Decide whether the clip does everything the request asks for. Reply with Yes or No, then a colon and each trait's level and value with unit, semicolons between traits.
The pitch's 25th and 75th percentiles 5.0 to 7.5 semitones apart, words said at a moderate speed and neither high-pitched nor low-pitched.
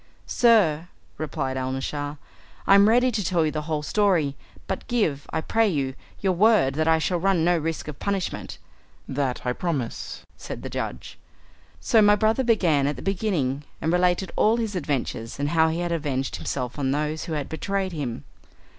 Yes: wide, 5.4 semitones; average, 180 wpm; medium, 160 Hz